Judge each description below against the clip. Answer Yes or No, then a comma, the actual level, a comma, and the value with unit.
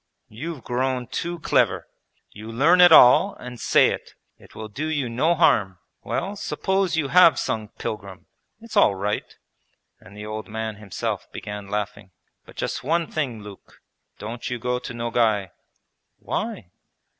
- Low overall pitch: Yes, low, 120 Hz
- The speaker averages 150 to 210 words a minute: Yes, average, 155 wpm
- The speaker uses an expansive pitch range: Yes, wide, 6.8 semitones